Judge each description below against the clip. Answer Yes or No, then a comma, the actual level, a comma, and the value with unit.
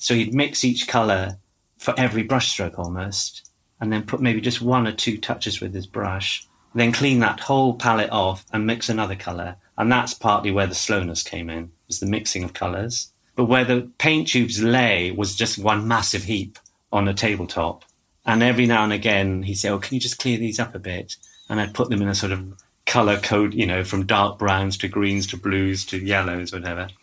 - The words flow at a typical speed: No, fast, 220 wpm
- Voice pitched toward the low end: Yes, low, 105 Hz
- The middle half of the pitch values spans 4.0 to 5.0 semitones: No, average, 3.5 semitones